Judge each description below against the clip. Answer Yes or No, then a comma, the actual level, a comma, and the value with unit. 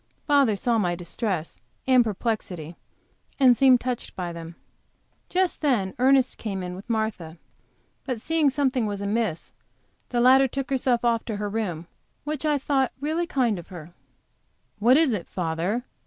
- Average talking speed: Yes, average, 160 wpm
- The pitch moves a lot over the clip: Yes, wide, 5.9 semitones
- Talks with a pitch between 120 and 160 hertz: No, high, 230 Hz